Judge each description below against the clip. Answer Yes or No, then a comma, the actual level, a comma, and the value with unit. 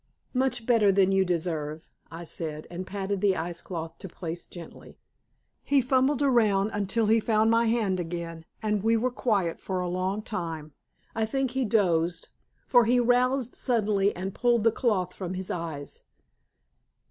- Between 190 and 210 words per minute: No, average, 165 wpm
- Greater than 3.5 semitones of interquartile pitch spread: Yes, average, 5.0 semitones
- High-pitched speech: Yes, high, 200 Hz